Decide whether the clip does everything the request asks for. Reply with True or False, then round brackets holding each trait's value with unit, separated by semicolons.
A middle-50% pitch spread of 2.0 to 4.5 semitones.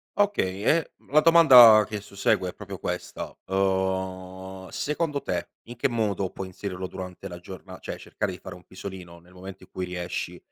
True (2.8 semitones)